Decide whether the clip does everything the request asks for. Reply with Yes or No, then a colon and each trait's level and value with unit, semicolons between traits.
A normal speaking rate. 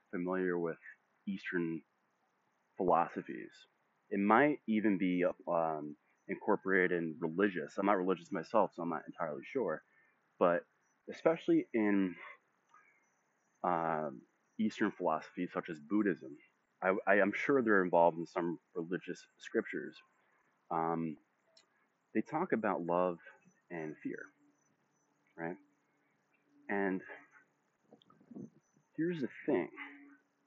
No: slow, 100 wpm